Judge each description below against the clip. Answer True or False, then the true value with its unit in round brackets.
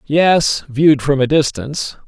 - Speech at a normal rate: True (145 wpm)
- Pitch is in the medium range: True (145 Hz)